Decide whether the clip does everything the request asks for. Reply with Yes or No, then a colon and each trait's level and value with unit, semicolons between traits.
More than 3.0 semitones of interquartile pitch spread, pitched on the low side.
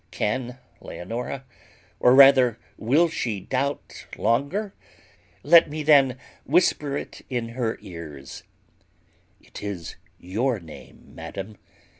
Yes: average, 5.1 semitones; low, 125 Hz